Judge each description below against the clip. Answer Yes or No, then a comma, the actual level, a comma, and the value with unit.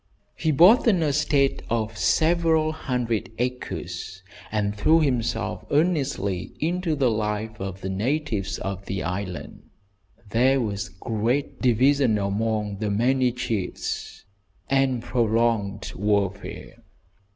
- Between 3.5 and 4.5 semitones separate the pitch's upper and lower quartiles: No, average, 5.2 semitones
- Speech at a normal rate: No, slow, 110 wpm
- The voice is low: Yes, low, 115 Hz